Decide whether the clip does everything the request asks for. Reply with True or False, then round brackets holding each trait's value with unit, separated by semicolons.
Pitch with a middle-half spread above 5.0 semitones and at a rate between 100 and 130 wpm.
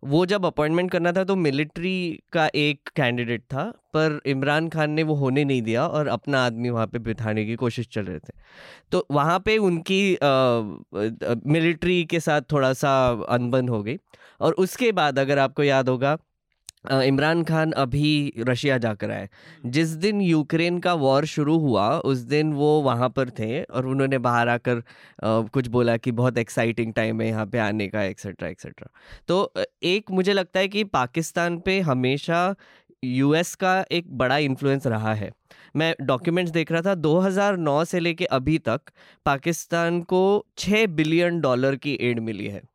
False (5.4 semitones; 170 wpm)